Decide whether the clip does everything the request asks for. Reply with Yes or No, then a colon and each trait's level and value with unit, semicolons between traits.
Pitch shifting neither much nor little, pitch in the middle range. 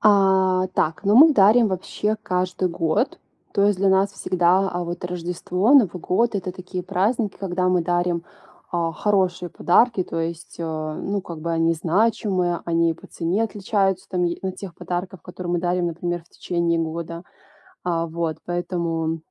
No: narrow, 2.3 semitones; medium, 180 Hz